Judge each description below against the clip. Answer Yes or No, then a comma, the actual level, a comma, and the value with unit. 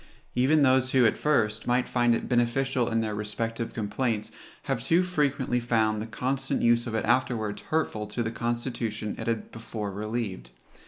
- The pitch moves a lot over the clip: No, average, 2.8 semitones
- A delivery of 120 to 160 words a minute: No, average, 170 wpm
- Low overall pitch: Yes, low, 120 Hz